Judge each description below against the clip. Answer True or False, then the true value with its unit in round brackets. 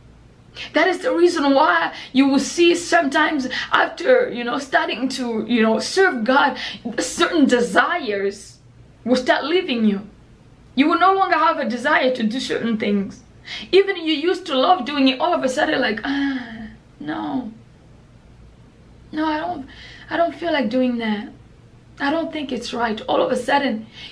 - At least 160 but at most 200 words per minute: True (170 wpm)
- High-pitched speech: True (275 Hz)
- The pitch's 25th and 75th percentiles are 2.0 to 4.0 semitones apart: False (5.5 semitones)